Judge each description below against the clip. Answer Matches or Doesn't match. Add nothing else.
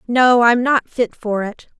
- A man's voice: Doesn't match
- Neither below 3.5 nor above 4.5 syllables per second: Matches